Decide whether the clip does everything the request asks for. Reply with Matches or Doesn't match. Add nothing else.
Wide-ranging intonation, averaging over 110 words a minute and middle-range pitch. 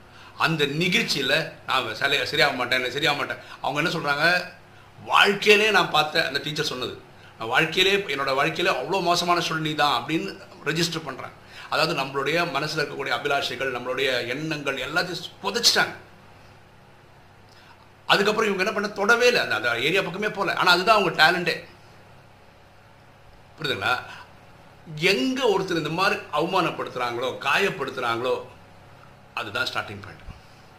Matches